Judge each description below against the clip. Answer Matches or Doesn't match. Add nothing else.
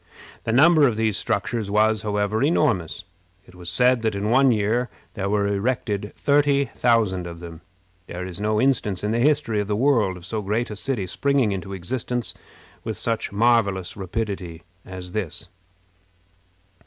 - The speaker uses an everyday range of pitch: Matches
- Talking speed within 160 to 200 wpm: Matches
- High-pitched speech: Doesn't match